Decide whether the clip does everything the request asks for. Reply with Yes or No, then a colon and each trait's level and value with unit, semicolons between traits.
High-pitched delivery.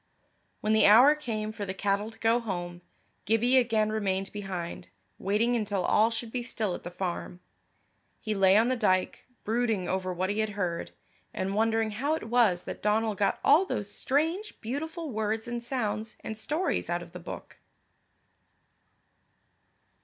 Yes: high, 215 Hz